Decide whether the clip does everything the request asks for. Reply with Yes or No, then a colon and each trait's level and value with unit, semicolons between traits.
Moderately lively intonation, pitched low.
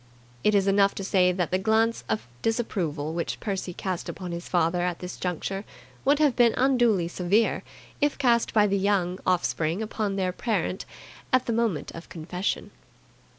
No: average, 4.0 semitones; high, 195 Hz